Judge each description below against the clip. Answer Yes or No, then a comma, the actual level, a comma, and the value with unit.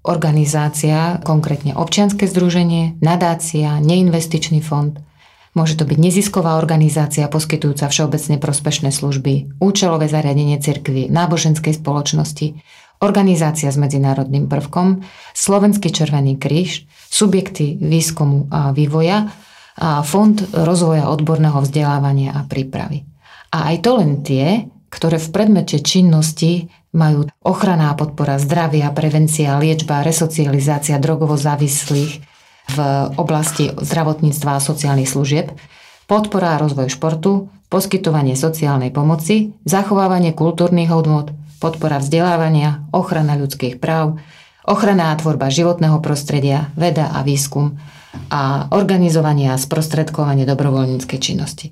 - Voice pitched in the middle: Yes, medium, 155 Hz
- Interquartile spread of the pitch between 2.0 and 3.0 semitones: Yes, average, 2.7 semitones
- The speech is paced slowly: Yes, slow, 105 wpm